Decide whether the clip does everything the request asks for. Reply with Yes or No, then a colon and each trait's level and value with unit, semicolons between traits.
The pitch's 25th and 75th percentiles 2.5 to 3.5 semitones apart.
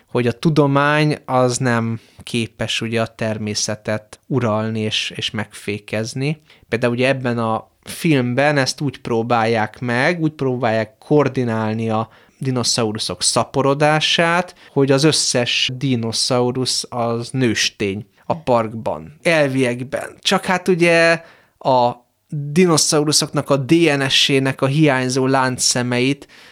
No: average, 4.1 semitones